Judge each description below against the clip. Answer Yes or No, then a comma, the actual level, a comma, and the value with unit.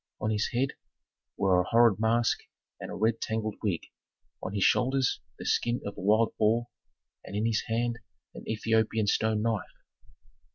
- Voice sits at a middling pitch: No, low, 110 Hz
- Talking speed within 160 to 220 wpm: Yes, average, 165 wpm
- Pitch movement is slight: Yes, narrow, 1.8 semitones